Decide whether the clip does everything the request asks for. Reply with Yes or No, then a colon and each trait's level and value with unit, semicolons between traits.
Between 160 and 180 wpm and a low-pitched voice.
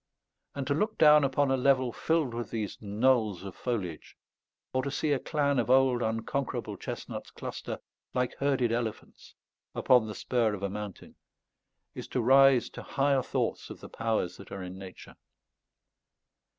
Yes: average, 165 wpm; low, 125 Hz